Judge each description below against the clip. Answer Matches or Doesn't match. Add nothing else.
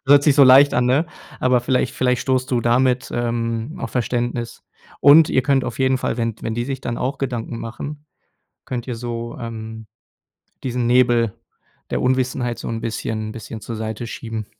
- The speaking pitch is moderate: Doesn't match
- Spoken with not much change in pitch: Matches